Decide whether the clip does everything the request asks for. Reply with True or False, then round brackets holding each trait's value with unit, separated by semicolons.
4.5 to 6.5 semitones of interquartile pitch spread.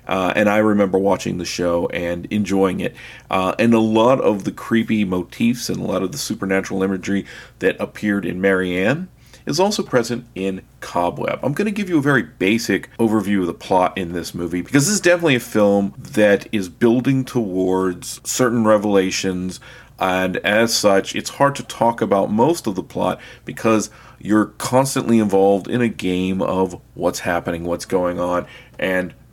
False (4.0 semitones)